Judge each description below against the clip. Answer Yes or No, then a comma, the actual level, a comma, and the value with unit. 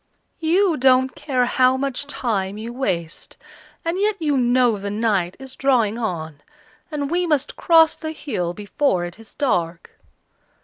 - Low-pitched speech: No, very high, 255 Hz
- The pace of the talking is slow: No, average, 150 wpm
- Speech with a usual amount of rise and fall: No, wide, 6.4 semitones